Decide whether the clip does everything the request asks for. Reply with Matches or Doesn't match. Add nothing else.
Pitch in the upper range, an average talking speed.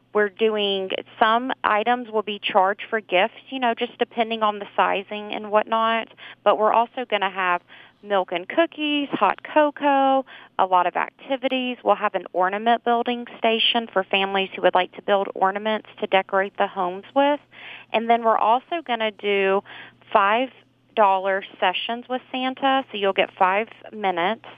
Matches